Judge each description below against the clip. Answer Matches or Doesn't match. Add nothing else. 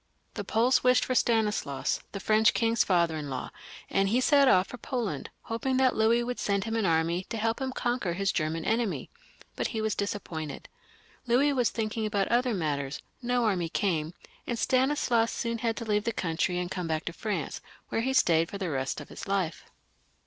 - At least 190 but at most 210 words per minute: Matches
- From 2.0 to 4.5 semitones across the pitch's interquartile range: Doesn't match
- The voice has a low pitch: Doesn't match